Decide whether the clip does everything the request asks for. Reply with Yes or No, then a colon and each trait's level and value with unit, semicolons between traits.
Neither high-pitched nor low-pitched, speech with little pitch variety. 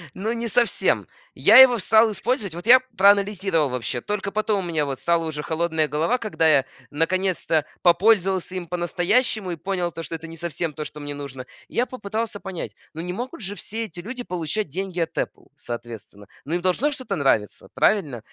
No: medium, 180 Hz; average, 4.9 semitones